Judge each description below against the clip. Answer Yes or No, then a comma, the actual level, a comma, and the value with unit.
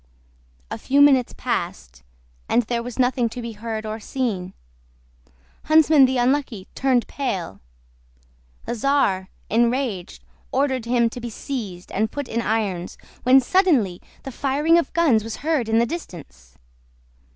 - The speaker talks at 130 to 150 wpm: Yes, average, 140 wpm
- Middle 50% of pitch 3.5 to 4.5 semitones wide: Yes, average, 4.1 semitones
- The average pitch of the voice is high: Yes, high, 240 Hz